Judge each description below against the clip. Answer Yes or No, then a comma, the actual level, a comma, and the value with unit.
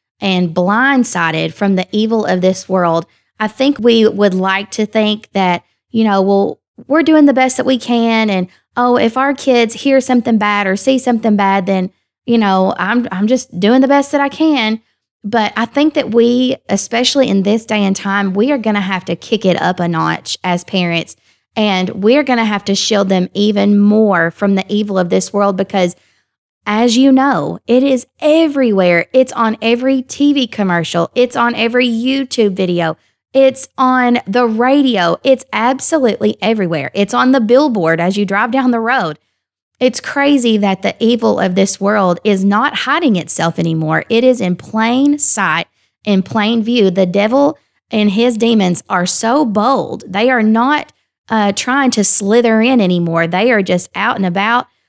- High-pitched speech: Yes, high, 220 Hz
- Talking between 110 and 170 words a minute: No, average, 185 wpm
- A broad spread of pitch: No, average, 4.5 semitones